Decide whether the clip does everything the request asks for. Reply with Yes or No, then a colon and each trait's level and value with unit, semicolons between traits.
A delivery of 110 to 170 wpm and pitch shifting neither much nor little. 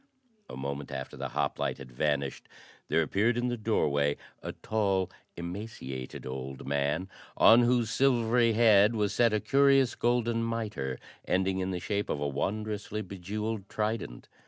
No: average, 150 wpm; wide, 7.9 semitones